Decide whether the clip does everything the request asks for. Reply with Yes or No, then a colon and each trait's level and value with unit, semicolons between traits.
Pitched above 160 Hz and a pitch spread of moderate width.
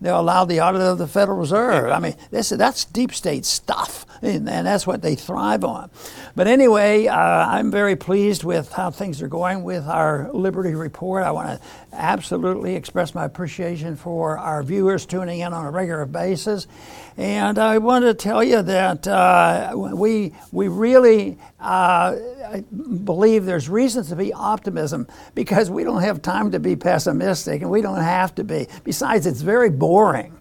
Yes: high, 190 Hz; average, 3.4 semitones